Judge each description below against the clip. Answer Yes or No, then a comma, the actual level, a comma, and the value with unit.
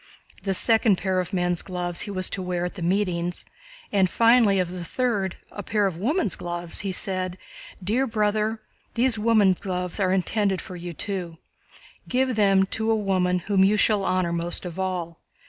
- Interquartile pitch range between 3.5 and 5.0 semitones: No, average, 2.9 semitones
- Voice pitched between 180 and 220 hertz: Yes, high, 190 Hz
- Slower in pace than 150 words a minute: No, average, 180 wpm